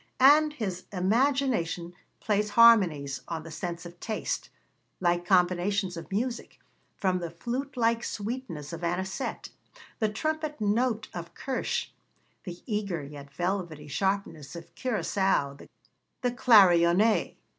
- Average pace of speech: No, slow, 120 wpm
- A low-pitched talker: No, high, 190 Hz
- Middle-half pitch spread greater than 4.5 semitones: Yes, average, 5.2 semitones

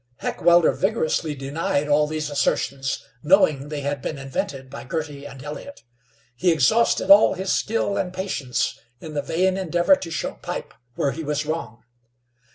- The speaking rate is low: No, average, 160 wpm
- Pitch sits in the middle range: Yes, medium, 150 Hz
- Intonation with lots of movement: No, average, 4.2 semitones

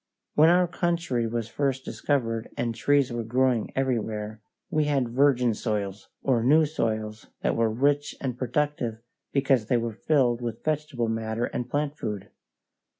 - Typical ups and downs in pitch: Yes, average, 4.1 semitones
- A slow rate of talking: No, average, 150 wpm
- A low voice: Yes, low, 125 Hz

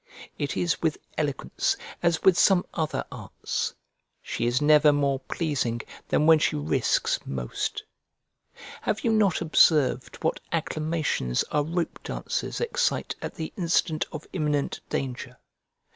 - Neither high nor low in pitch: Yes, medium, 155 Hz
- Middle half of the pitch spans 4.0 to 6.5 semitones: No, average, 3.6 semitones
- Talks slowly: Yes, slow, 130 wpm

